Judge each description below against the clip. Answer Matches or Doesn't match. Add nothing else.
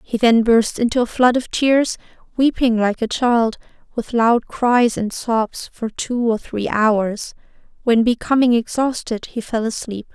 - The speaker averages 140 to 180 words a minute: Matches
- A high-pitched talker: Matches